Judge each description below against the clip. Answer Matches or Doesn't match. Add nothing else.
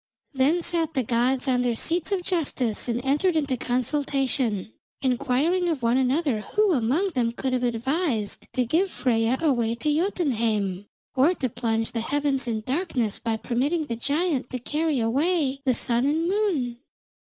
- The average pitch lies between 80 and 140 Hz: Doesn't match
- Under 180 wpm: Matches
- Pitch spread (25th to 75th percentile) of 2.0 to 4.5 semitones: Doesn't match